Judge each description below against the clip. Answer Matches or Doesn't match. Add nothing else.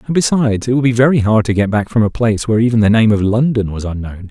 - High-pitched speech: Doesn't match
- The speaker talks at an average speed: Doesn't match